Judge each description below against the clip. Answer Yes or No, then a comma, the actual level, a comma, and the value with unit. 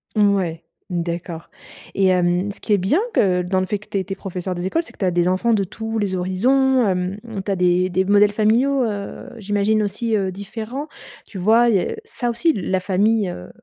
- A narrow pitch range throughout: No, average, 3.3 semitones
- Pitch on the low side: No, high, 200 Hz